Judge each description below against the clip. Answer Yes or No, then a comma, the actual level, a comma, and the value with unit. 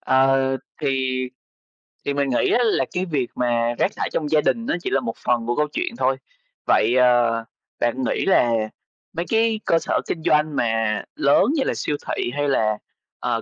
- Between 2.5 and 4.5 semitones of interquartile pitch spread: Yes, average, 4.2 semitones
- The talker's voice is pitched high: No, low, 135 Hz